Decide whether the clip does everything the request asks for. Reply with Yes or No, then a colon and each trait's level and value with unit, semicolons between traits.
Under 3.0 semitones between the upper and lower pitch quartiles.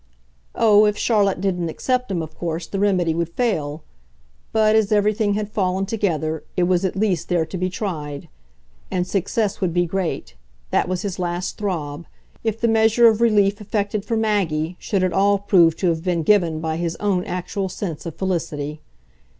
No: average, 3.6 semitones